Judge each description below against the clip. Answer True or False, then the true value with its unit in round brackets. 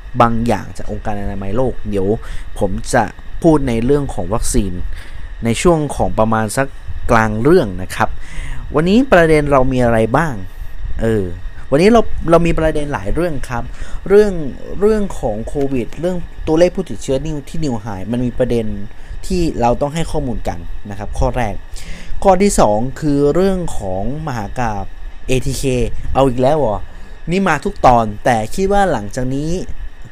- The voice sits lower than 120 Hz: False (125 Hz)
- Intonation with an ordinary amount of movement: False (6.7 semitones)